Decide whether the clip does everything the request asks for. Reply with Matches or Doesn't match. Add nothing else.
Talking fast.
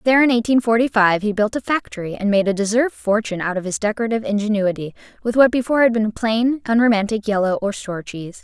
Matches